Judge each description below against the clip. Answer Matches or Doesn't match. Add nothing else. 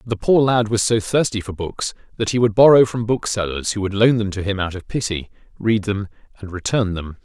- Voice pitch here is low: Matches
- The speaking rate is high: Matches